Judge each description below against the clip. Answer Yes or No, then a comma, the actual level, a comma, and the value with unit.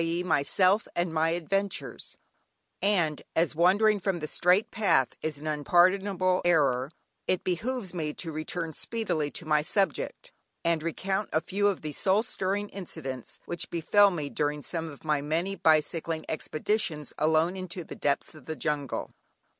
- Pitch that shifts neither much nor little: Yes, average, 3.8 semitones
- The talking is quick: No, average, 155 wpm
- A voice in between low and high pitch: Yes, medium, 170 Hz